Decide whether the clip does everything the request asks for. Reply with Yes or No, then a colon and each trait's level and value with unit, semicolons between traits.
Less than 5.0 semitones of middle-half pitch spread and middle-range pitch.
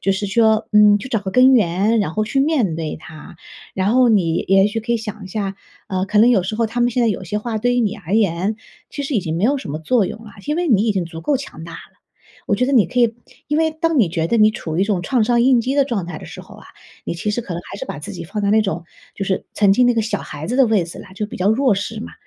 No: average, 4.2 semitones; high, 210 Hz